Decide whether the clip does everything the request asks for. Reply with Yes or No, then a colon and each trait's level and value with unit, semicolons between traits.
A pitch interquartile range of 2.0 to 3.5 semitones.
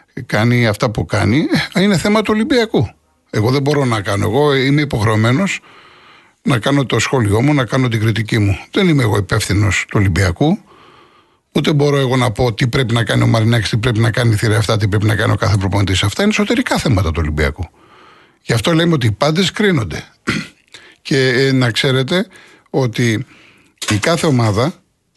No: wide, 5.4 semitones